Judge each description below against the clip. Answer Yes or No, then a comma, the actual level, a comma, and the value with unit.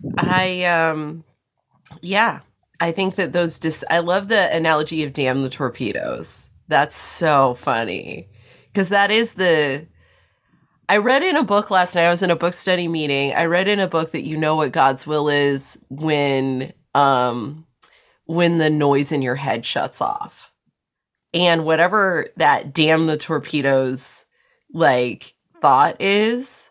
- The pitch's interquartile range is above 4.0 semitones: Yes, average, 4.4 semitones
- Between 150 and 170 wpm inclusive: Yes, average, 155 wpm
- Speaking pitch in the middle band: Yes, medium, 160 Hz